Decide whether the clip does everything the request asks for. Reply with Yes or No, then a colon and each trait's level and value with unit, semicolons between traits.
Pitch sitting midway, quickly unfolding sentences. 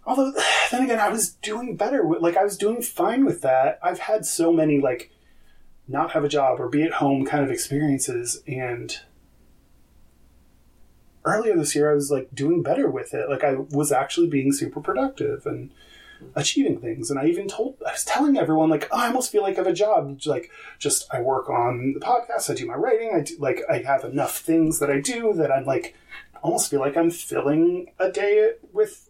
Yes: medium, 170 Hz; fast, 210 wpm